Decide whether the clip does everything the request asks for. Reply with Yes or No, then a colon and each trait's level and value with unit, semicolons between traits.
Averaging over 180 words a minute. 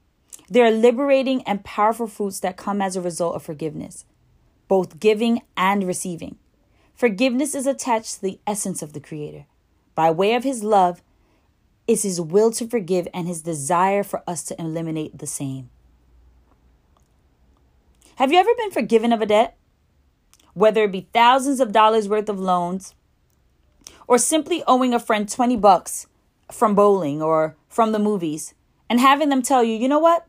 No: average, 165 wpm